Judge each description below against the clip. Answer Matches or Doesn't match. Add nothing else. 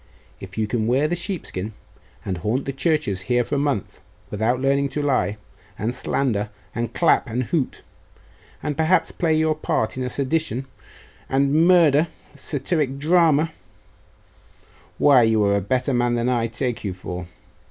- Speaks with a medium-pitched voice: Doesn't match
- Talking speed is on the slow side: Doesn't match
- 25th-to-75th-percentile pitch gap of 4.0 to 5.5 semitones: Matches